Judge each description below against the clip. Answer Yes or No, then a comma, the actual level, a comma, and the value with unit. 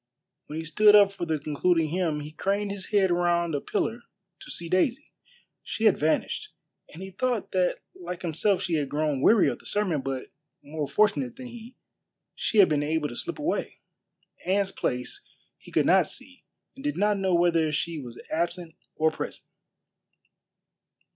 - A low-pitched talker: No, medium, 175 Hz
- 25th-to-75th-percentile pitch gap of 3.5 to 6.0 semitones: Yes, average, 4.7 semitones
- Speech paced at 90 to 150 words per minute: No, average, 175 wpm